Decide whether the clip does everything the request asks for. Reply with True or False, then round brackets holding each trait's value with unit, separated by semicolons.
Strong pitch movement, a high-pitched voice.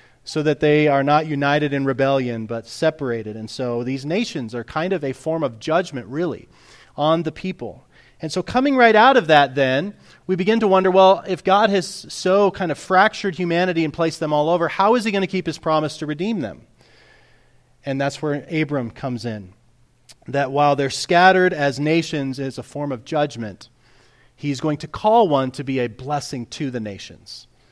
False (5.7 semitones; 145 Hz)